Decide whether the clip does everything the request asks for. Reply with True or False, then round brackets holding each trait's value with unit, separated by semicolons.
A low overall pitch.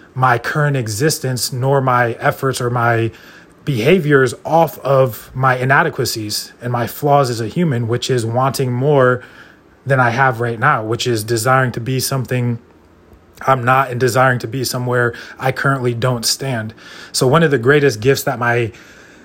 True (130 Hz)